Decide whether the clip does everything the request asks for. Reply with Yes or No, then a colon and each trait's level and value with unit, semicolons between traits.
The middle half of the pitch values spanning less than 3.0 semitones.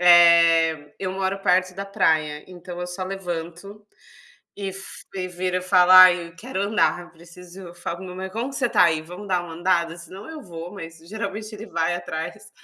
Yes: narrow, 2.4 semitones